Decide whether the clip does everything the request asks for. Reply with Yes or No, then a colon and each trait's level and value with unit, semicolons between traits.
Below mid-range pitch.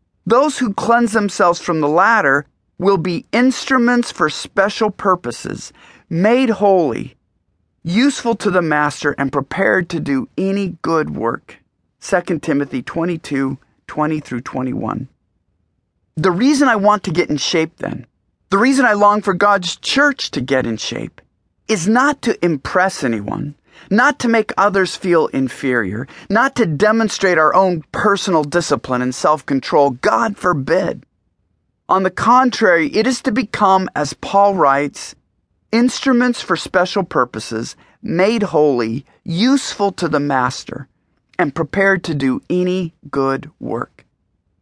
No: medium, 180 Hz